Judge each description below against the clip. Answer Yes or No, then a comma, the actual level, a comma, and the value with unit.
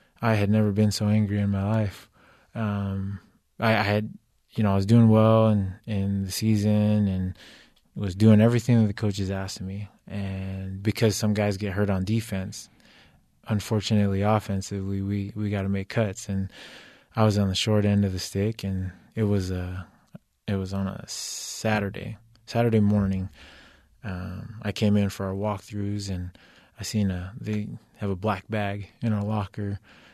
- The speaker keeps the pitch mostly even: Yes, narrow, 1.7 semitones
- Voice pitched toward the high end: No, low, 105 Hz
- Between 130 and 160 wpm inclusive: No, average, 175 wpm